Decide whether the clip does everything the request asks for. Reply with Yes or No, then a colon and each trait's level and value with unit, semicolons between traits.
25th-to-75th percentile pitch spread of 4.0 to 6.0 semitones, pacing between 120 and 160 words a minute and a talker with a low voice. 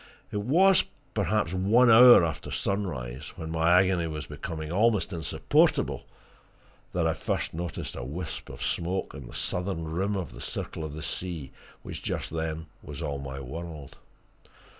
No: average, 3.6 semitones; average, 155 wpm; very low, 85 Hz